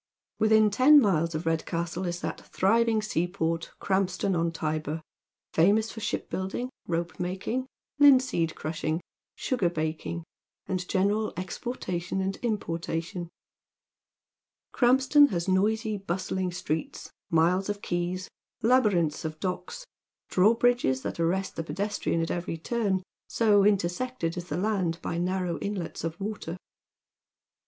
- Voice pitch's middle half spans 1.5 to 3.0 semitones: No, average, 4.2 semitones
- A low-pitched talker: No, medium, 185 Hz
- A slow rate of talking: Yes, slow, 115 wpm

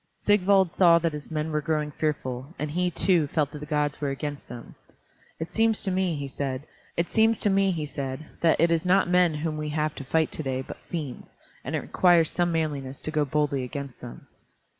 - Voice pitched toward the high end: No, medium, 155 Hz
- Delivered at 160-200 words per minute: Yes, average, 195 wpm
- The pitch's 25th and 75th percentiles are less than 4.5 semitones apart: Yes, average, 3.2 semitones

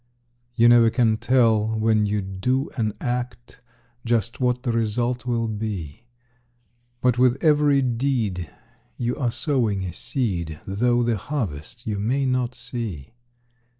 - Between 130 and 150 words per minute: Yes, slow, 135 wpm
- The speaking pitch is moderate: No, low, 120 Hz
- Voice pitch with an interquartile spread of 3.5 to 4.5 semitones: No, average, 2.8 semitones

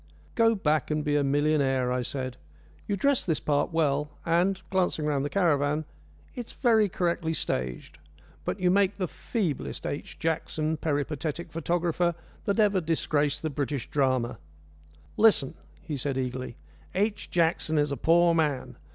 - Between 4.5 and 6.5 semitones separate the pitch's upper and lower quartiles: No, average, 3.8 semitones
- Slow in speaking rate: No, average, 150 wpm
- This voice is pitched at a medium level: Yes, medium, 155 Hz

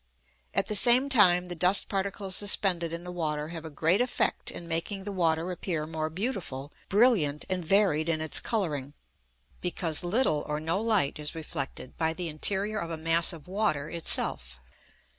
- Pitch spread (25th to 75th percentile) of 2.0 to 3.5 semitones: No, average, 3.9 semitones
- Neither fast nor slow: Yes, average, 175 wpm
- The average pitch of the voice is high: No, medium, 170 Hz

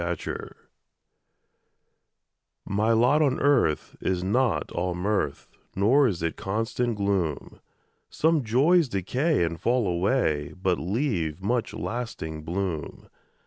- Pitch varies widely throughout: Yes, wide, 6.1 semitones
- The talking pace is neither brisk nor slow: No, slow, 115 wpm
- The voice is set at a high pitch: No, low, 100 Hz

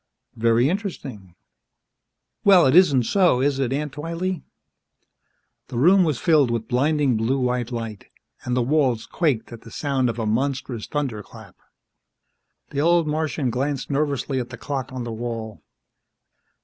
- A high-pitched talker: No, low, 130 Hz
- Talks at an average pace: Yes, average, 150 wpm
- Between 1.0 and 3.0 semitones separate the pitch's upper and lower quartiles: No, average, 4.2 semitones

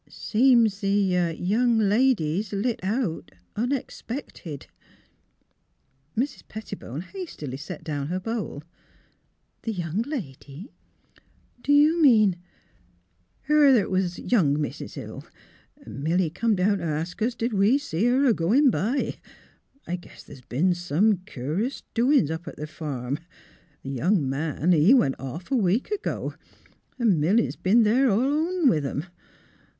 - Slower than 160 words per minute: Yes, average, 145 wpm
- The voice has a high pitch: Yes, high, 195 Hz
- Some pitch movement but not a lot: No, wide, 7.4 semitones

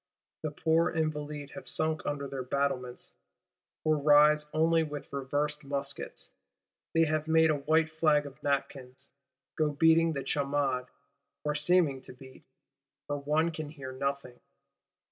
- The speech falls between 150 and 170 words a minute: No, average, 140 wpm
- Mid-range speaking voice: Yes, medium, 150 Hz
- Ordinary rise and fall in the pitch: No, narrow, 2.2 semitones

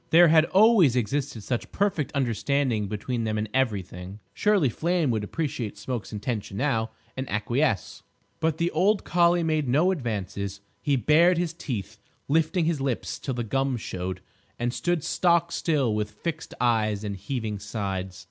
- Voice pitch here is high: No, low, 130 Hz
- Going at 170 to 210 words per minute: No, average, 155 wpm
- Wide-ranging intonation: Yes, wide, 7.2 semitones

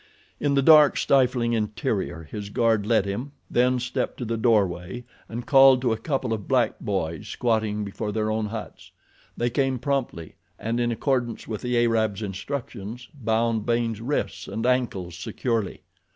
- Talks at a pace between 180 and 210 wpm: No, average, 160 wpm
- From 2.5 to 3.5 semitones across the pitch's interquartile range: Yes, average, 3.0 semitones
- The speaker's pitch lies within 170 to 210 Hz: No, low, 115 Hz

